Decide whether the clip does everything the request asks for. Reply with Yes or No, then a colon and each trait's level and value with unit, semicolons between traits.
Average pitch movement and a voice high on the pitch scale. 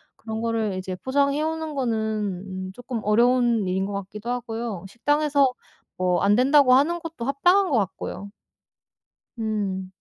No: wide, 5.7 semitones; high, 235 Hz